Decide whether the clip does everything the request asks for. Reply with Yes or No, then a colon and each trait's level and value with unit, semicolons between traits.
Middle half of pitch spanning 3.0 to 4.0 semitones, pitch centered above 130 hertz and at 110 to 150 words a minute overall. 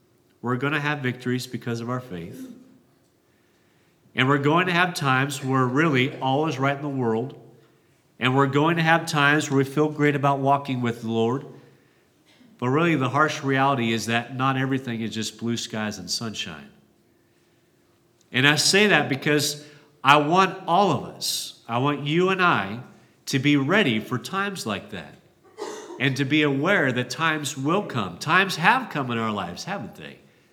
No: average, 3.7 semitones; medium, 140 Hz; average, 180 wpm